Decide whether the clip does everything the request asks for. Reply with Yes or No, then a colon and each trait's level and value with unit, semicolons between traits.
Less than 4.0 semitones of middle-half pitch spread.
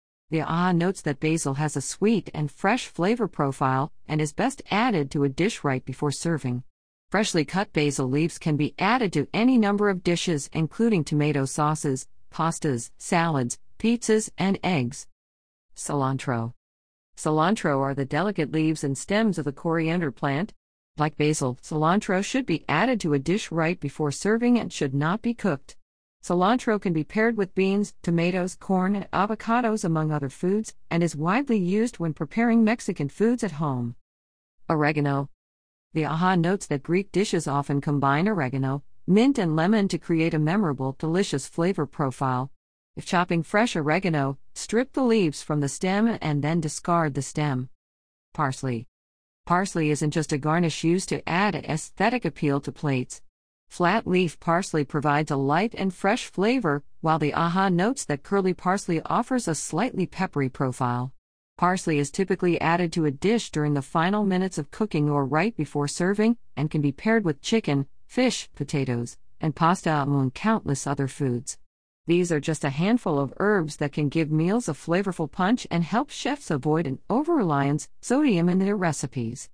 No: average, 5.3 semitones